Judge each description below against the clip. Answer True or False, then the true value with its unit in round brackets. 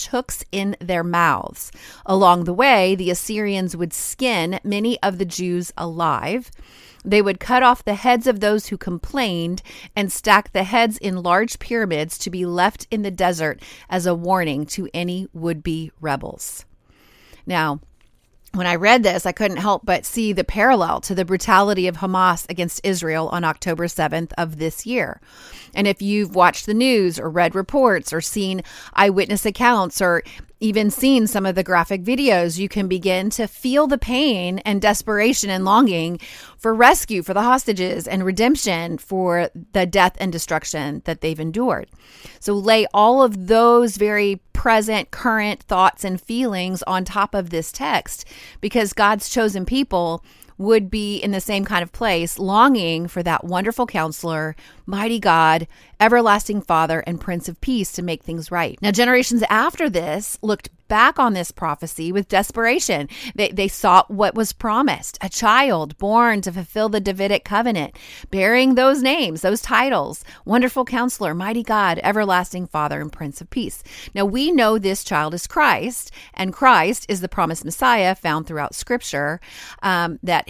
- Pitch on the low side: False (195 Hz)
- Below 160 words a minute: False (165 wpm)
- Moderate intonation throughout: True (4.1 semitones)